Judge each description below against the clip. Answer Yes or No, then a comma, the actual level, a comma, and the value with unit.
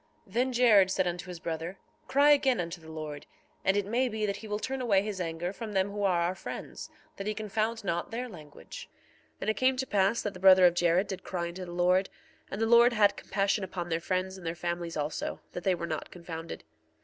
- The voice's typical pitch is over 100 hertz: Yes, high, 190 Hz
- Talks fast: Yes, fast, 240 wpm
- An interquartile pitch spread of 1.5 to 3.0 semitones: No, average, 3.8 semitones